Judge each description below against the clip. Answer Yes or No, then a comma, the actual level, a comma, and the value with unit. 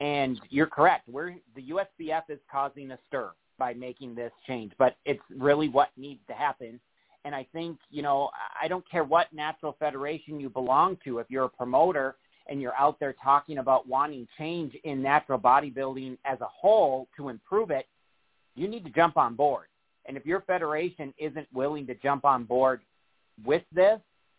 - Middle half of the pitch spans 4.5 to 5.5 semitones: No, average, 2.8 semitones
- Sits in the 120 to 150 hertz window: Yes, medium, 140 Hz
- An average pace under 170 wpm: No, average, 180 wpm